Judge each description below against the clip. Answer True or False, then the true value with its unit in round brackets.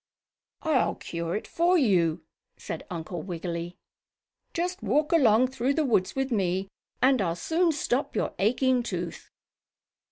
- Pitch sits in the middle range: False (225 Hz)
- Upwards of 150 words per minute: False (135 wpm)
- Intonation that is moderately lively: False (7.8 semitones)